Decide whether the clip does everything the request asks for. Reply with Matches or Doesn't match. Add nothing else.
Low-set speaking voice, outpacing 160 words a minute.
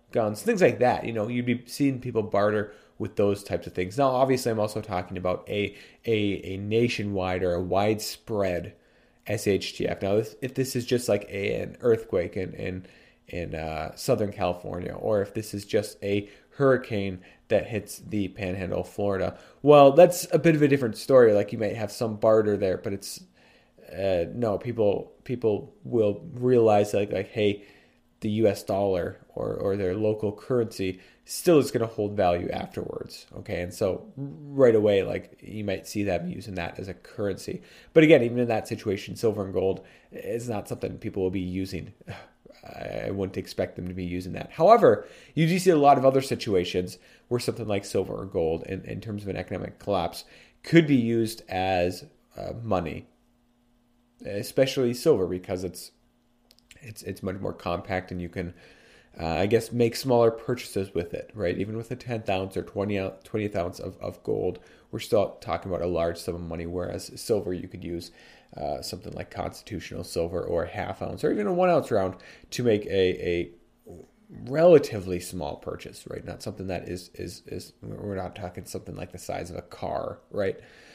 Matches